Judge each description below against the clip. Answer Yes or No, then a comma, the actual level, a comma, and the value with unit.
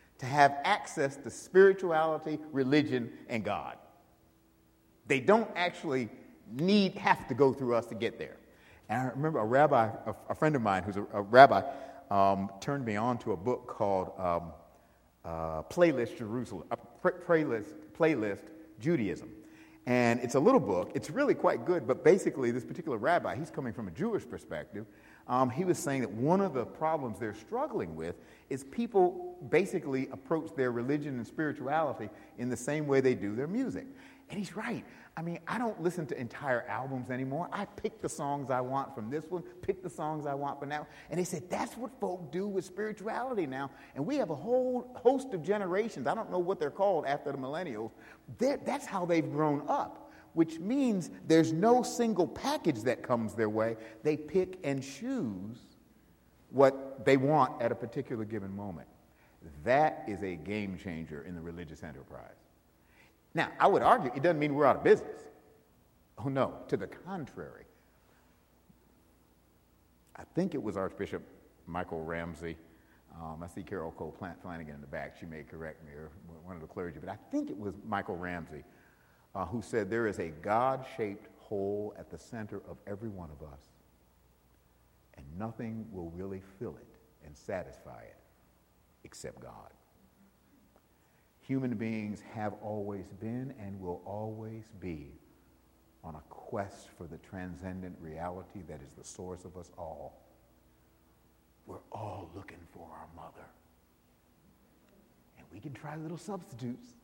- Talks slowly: No, average, 170 wpm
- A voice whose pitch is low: Yes, low, 115 Hz